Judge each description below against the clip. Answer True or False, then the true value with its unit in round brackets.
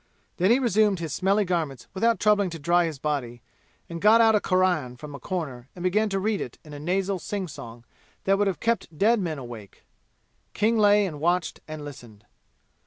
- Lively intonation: True (5.7 semitones)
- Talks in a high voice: False (180 Hz)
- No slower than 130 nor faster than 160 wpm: False (195 wpm)